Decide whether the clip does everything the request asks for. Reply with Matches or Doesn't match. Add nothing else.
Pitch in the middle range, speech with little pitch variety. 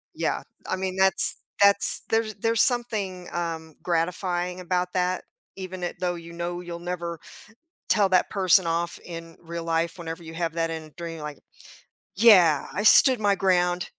Matches